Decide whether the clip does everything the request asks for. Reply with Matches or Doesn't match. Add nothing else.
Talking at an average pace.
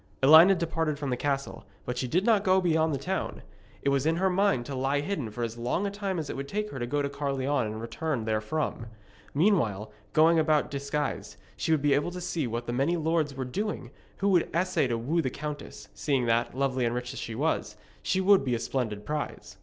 Doesn't match